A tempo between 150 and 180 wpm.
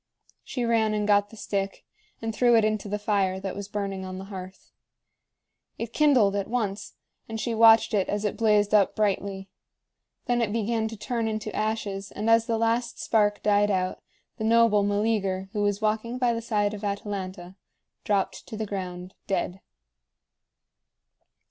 Yes: average, 170 wpm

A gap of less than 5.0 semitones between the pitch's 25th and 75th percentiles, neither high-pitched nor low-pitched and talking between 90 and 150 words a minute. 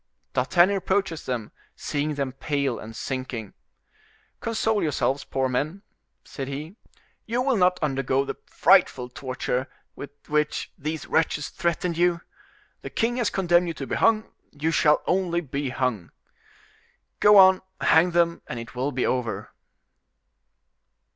No: average, 5.3 semitones; medium, 150 Hz; average, 140 wpm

